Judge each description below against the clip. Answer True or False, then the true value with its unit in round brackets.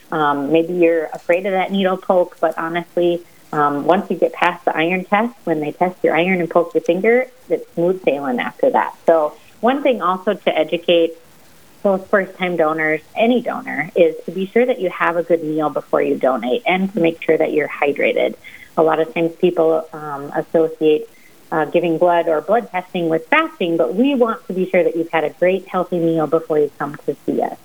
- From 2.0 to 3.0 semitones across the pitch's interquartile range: True (2.6 semitones)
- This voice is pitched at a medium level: True (170 Hz)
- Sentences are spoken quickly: True (210 wpm)